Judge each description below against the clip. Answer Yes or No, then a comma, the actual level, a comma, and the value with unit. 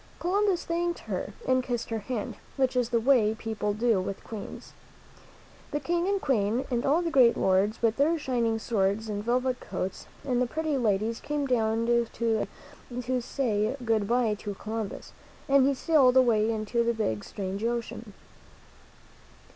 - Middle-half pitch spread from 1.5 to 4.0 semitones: Yes, average, 3.4 semitones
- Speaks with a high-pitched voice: Yes, high, 235 Hz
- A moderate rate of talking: Yes, average, 165 wpm